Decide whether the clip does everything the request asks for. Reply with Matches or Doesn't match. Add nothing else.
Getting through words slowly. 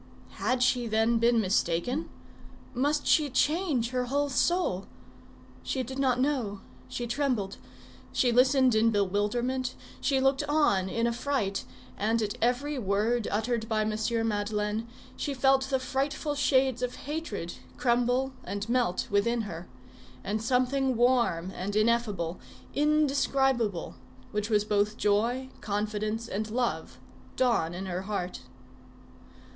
Matches